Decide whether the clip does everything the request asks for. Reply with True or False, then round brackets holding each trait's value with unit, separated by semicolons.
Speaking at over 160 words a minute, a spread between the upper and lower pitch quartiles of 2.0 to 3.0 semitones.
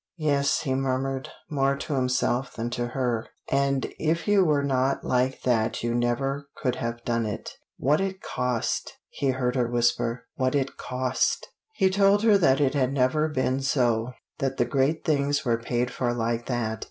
True (180 wpm; 2.7 semitones)